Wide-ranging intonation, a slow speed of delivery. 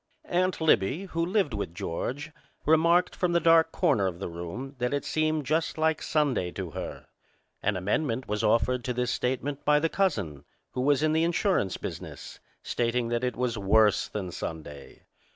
No: wide, 7.2 semitones; average, 175 wpm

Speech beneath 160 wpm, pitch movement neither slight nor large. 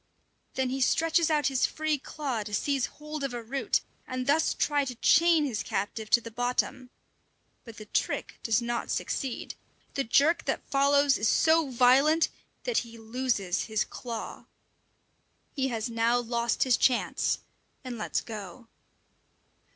Yes: average, 150 wpm; average, 3.7 semitones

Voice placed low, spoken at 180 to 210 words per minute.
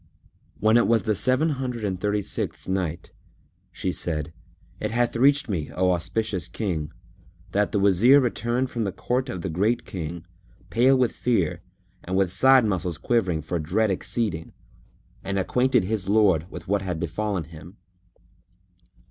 No: low, 100 Hz; average, 155 wpm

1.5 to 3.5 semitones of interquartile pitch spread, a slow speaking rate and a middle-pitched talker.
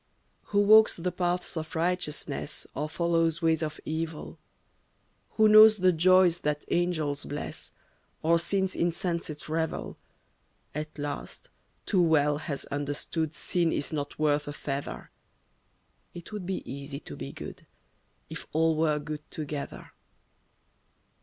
Yes: average, 2.9 semitones; slow, 130 wpm; medium, 160 Hz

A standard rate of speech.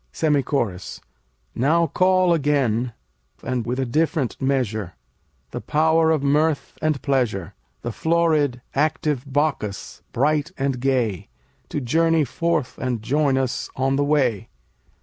No: slow, 130 wpm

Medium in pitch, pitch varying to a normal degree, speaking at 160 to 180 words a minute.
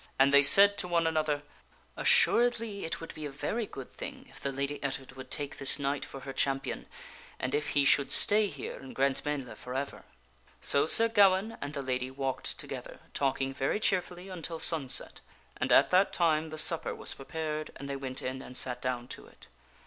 No: medium, 145 Hz; average, 3.7 semitones; average, 195 wpm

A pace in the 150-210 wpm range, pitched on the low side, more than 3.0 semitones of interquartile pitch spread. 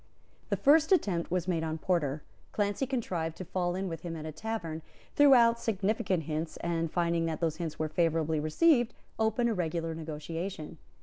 No: average, 180 wpm; medium, 170 Hz; average, 4.9 semitones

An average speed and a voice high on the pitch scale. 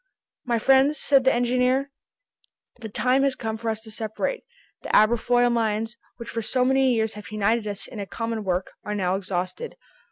Yes: average, 185 wpm; high, 230 Hz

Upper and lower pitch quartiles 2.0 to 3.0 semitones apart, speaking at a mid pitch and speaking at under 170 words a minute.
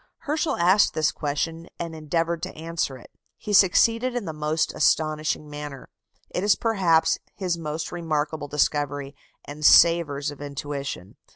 Yes: average, 2.7 semitones; medium, 155 Hz; average, 145 wpm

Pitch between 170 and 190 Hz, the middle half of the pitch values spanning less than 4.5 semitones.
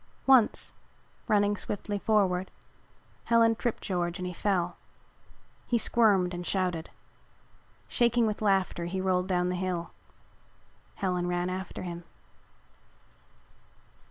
Yes: medium, 185 Hz; average, 2.9 semitones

